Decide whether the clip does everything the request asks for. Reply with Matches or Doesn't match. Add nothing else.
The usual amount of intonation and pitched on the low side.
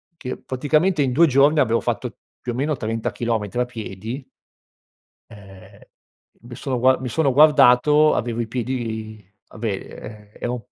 Matches